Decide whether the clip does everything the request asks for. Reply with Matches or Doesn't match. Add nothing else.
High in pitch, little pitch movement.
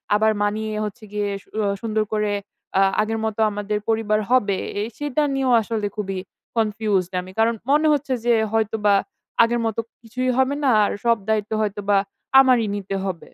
Matches